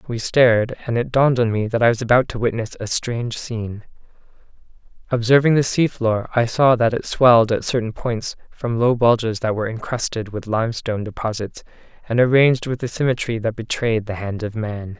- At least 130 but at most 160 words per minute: No, average, 190 wpm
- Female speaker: No, male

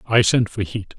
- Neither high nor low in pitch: No, low, 105 Hz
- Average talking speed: No, fast, 245 wpm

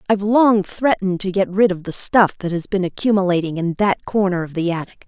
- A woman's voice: Yes, female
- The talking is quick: Yes, fast, 225 wpm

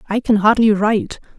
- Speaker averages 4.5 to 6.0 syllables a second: Yes, 5.8 syllables/s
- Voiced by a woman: Yes, female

